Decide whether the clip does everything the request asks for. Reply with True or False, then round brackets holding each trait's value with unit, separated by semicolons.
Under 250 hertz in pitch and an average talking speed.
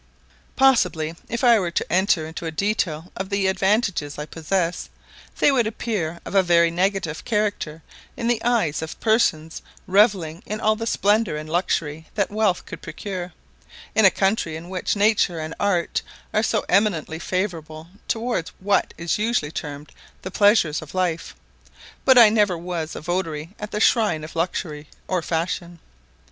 True (185 Hz; 165 wpm)